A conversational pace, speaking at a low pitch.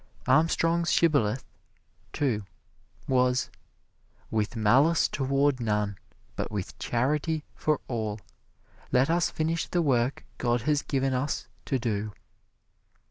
No: slow, 110 wpm; low, 130 Hz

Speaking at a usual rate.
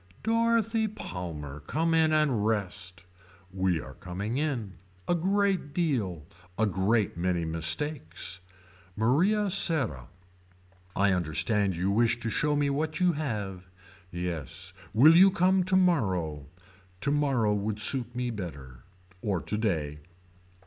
No: slow, 120 wpm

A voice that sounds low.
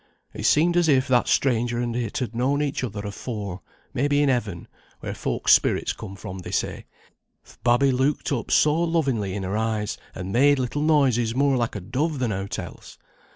Yes: low, 125 Hz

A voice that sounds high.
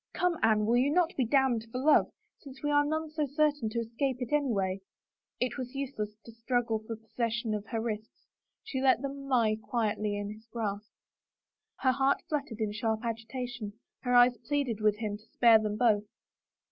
Yes: high, 235 Hz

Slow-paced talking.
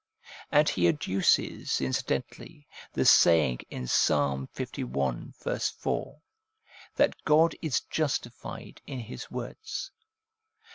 Yes: slow, 95 wpm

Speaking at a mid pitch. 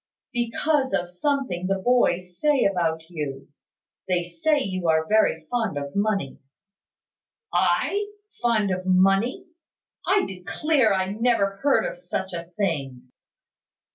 No: high, 195 Hz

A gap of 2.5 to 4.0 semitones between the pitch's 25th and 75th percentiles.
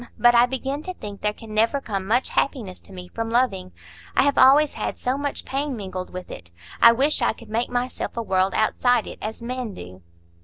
No: average, 4.5 semitones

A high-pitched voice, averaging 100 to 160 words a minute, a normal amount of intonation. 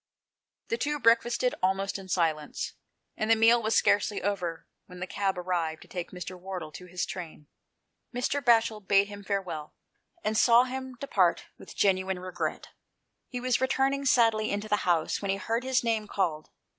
No: high, 200 Hz; average, 170 wpm; average, 4.3 semitones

